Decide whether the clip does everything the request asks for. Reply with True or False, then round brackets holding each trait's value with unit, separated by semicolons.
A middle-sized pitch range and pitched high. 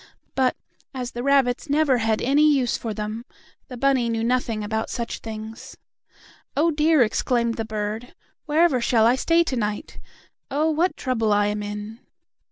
True (4.0 semitones; 240 Hz)